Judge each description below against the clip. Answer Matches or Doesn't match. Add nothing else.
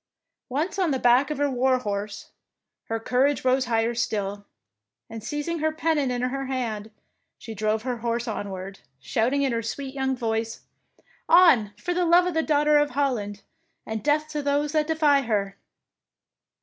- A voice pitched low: Doesn't match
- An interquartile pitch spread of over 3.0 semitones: Matches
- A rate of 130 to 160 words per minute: Doesn't match